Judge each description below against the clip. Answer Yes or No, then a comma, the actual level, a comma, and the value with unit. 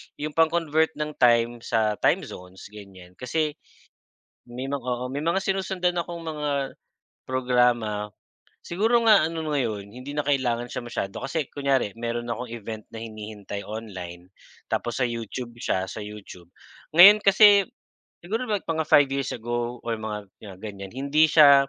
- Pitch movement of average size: No, wide, 6.1 semitones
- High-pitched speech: No, low, 125 Hz